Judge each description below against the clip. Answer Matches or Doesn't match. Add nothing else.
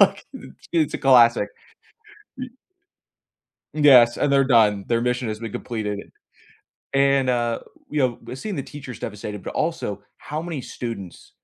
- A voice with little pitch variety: Doesn't match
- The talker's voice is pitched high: Doesn't match